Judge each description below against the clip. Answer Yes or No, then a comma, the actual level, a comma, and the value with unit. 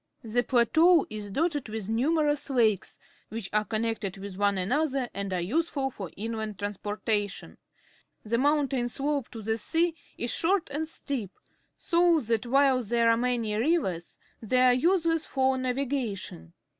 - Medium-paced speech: Yes, average, 150 wpm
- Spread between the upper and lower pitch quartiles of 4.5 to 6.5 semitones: Yes, average, 5.1 semitones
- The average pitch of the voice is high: Yes, high, 240 Hz